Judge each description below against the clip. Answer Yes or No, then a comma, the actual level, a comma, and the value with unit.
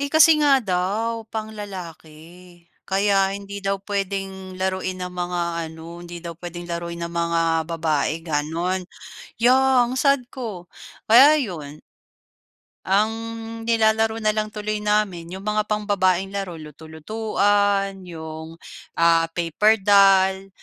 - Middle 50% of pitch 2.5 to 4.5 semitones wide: Yes, average, 3.7 semitones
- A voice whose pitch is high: Yes, high, 195 Hz